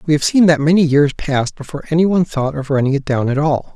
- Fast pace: Yes, fast, 270 wpm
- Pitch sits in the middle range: Yes, medium, 150 Hz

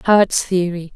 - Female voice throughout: Yes, female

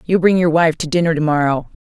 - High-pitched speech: No, medium, 165 Hz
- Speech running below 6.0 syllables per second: No, 6.1 syllables/s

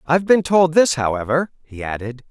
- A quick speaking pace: No, average, 180 wpm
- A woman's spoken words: No, male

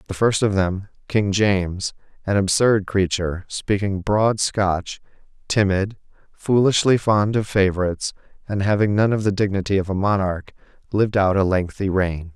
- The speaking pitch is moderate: No, low, 100 Hz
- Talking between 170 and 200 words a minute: No, average, 150 wpm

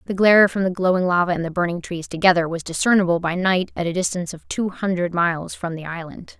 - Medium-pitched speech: Yes, medium, 180 Hz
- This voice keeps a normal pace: No, fast, 235 wpm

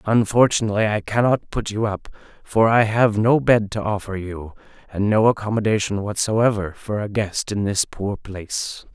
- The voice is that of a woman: No, male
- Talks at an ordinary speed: Yes, average, 170 wpm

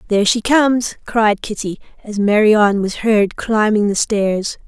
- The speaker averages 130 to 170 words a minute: Yes, average, 155 wpm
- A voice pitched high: Yes, high, 215 Hz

